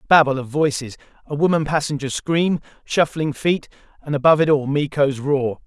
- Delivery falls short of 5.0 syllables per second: No, 5.4 syllables/s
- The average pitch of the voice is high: No, medium, 145 Hz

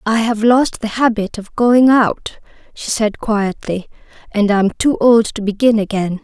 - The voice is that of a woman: Yes, female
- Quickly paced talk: No, average, 175 wpm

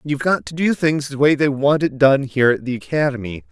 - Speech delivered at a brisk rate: Yes, fast, 255 wpm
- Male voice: Yes, male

